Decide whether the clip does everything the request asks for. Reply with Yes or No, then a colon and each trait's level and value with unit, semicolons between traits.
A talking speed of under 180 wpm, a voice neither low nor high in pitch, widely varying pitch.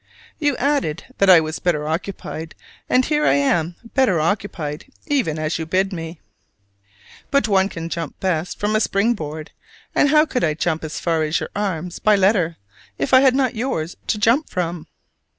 No: average, 185 wpm; medium, 180 Hz; wide, 6.1 semitones